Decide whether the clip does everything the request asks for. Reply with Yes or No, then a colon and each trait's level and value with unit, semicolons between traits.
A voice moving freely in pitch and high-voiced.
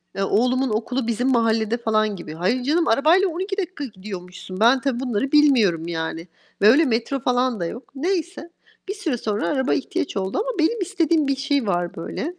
Yes: wide, 6.5 semitones; very high, 250 Hz